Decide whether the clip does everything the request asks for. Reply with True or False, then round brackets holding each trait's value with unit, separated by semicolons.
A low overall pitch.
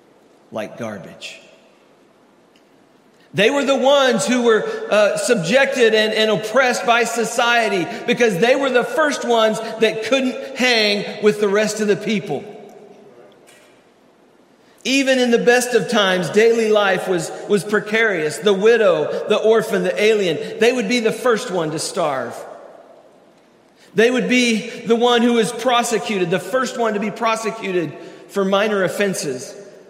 False (220 Hz)